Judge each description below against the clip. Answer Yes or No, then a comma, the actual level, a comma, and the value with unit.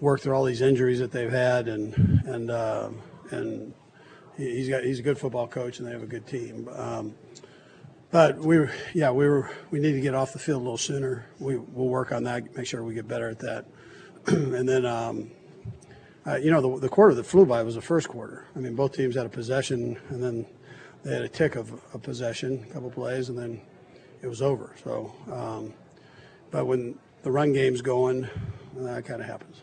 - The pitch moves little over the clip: Yes, narrow, 2.2 semitones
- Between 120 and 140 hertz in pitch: Yes, low, 130 Hz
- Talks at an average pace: No, fast, 215 wpm